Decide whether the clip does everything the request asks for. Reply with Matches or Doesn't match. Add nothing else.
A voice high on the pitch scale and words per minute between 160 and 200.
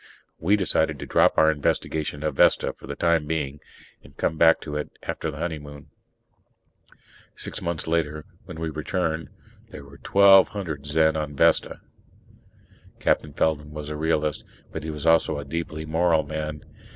Doesn't match